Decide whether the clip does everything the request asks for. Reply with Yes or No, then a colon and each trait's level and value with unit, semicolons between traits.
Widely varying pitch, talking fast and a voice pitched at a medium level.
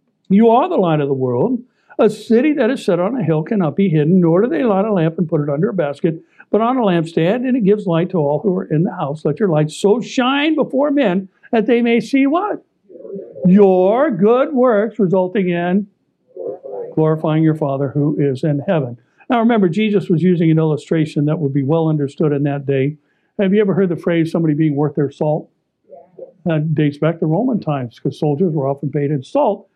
Yes: wide, 5.9 semitones; fast, 220 wpm; medium, 180 Hz